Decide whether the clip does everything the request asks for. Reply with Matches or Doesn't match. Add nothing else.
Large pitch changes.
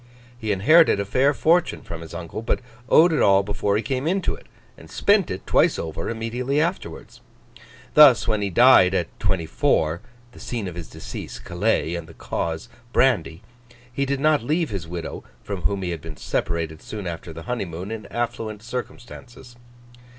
Matches